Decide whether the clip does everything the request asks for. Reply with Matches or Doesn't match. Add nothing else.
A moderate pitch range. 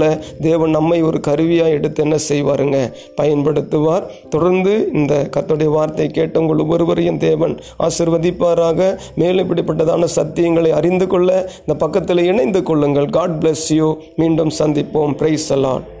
Doesn't match